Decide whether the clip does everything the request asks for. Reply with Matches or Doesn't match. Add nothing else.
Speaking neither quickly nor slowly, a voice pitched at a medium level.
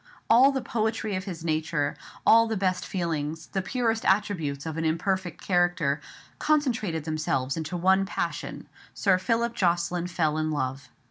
Matches